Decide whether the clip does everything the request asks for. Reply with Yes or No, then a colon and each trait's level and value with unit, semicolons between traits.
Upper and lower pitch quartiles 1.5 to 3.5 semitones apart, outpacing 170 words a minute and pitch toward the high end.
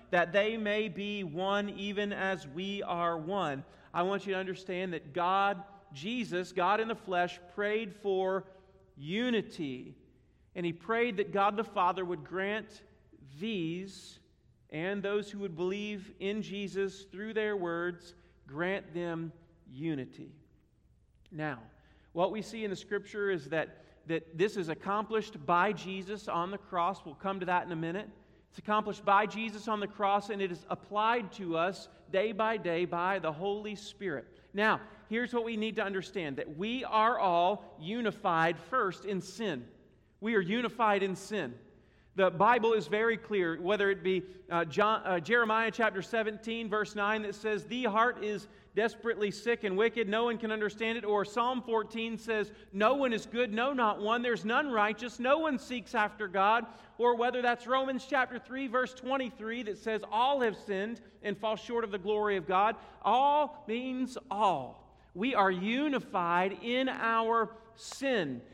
No: average, 3.1 semitones; average, 165 wpm; high, 205 Hz